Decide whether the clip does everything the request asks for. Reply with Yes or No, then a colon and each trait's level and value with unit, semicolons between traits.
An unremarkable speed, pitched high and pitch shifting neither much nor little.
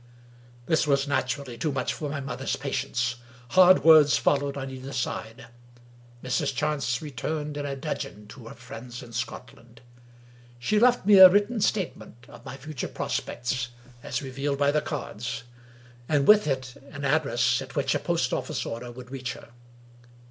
No: average, 165 wpm; medium, 140 Hz; average, 3.5 semitones